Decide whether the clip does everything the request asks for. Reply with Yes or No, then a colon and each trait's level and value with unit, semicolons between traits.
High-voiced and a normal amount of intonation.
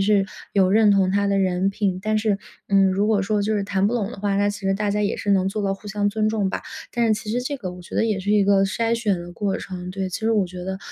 No: high, 200 Hz; narrow, 1.7 semitones